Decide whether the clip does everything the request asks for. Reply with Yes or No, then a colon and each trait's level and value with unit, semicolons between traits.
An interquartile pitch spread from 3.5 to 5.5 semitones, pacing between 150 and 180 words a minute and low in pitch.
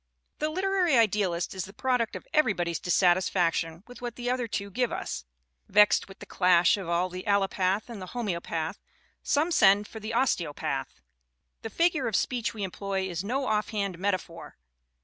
No: average, 4.8 semitones; average, 170 wpm; high, 200 Hz